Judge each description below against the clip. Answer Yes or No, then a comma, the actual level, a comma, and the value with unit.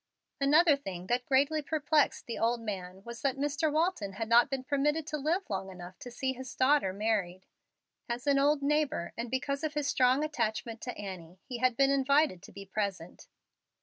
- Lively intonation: Yes, wide, 5.7 semitones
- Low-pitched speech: No, very high, 255 Hz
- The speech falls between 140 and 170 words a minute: No, average, 190 wpm